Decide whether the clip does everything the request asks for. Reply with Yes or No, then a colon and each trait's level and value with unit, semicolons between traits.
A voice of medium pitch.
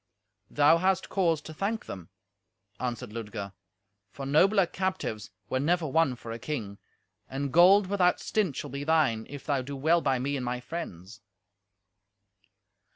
Yes: medium, 145 Hz